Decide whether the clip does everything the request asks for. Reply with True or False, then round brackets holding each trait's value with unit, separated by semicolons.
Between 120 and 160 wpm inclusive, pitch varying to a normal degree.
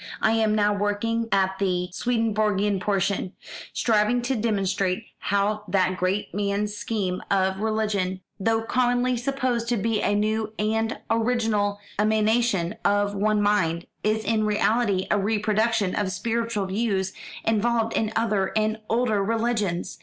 False (135 wpm; 2.2 semitones)